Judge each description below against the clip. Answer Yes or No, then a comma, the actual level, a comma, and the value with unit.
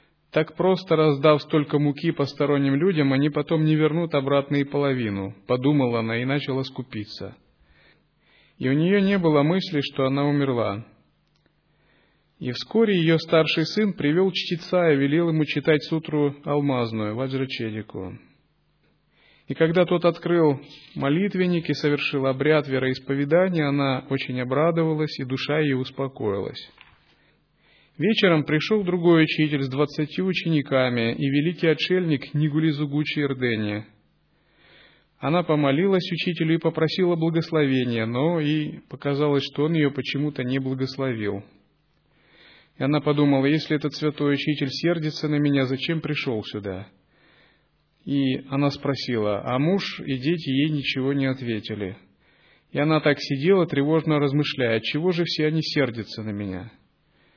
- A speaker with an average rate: Yes, average, 125 wpm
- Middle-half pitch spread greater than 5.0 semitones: No, average, 3.4 semitones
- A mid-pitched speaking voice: Yes, medium, 145 Hz